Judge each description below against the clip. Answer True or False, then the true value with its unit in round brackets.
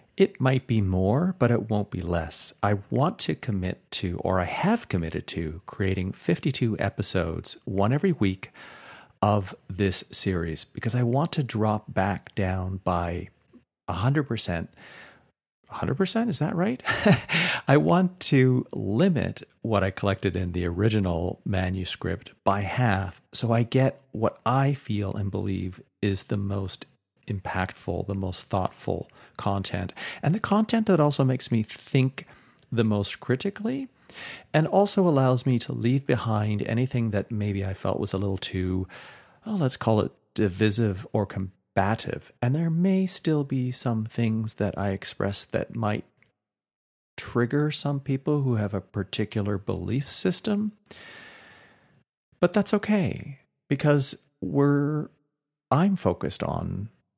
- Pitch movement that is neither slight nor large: False (6.5 semitones)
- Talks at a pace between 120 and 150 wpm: True (140 wpm)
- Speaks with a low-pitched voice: True (115 Hz)